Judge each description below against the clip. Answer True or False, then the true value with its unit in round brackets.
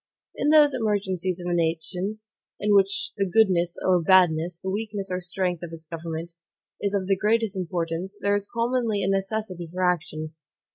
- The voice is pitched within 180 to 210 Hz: True (185 Hz)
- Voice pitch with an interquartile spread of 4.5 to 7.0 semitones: False (2.9 semitones)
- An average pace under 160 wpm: False (175 wpm)